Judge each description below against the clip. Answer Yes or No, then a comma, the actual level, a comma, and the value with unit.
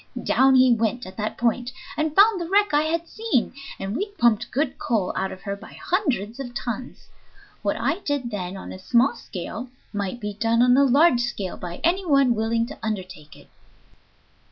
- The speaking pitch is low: No, high, 240 Hz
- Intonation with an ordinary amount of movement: No, wide, 5.7 semitones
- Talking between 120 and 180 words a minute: No, average, 195 wpm